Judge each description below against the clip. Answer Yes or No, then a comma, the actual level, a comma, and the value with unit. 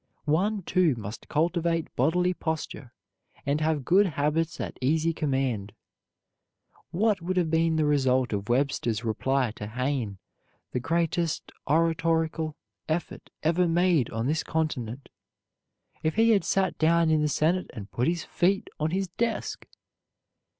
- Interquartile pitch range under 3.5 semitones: No, average, 4.3 semitones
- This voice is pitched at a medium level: Yes, medium, 160 Hz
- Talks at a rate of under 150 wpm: Yes, average, 140 wpm